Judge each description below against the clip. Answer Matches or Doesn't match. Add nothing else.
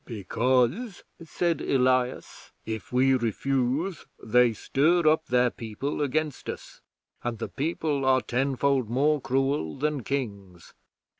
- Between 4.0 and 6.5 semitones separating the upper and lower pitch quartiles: Doesn't match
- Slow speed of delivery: Matches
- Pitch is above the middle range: Doesn't match